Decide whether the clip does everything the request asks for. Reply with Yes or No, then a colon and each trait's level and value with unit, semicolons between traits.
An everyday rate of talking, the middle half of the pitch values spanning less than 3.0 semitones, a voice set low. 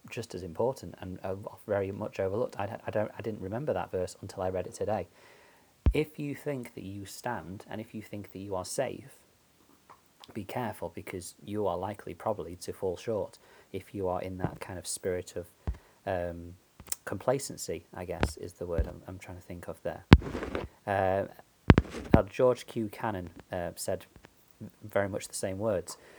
Yes: average, 180 wpm; narrow, 2.6 semitones; very low, 95 Hz